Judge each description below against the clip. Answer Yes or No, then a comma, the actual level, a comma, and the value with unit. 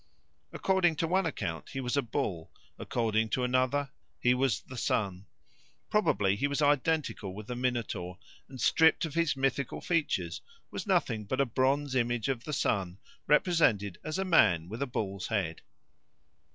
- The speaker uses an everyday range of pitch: No, wide, 5.7 semitones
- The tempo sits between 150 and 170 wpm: Yes, average, 165 wpm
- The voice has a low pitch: Yes, low, 130 Hz